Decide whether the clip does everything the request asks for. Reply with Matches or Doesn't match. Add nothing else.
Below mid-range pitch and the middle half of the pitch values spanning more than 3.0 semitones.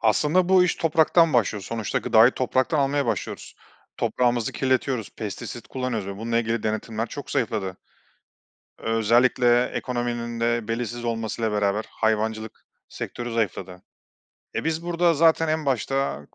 Matches